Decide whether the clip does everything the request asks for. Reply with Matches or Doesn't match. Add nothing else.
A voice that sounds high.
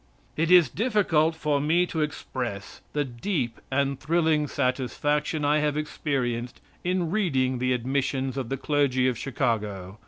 Doesn't match